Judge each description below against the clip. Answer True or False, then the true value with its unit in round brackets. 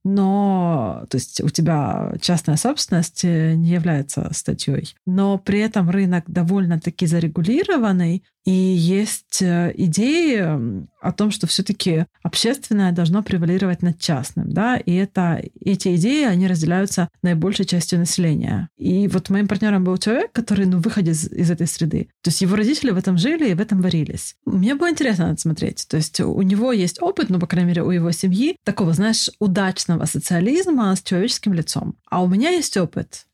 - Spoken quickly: True (165 wpm)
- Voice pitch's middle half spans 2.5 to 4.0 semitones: True (3.0 semitones)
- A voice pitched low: False (185 Hz)